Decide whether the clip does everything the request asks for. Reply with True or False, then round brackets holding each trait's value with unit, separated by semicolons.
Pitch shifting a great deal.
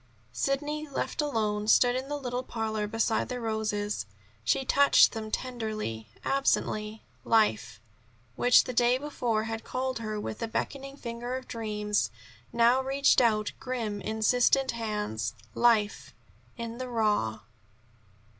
False (3.1 semitones)